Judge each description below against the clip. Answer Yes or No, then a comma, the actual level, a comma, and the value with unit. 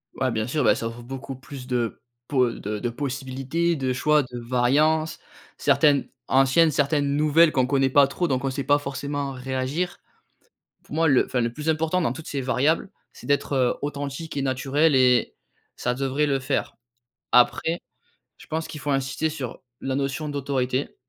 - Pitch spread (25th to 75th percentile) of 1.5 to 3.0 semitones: Yes, average, 2.7 semitones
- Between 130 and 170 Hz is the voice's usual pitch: Yes, low, 135 Hz